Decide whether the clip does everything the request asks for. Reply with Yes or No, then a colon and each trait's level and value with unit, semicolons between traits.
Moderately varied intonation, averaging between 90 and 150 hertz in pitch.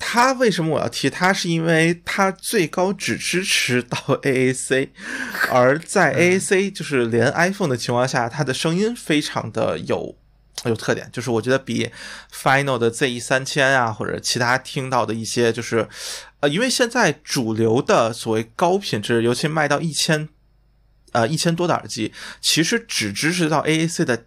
No: wide, 5.8 semitones; medium, 140 Hz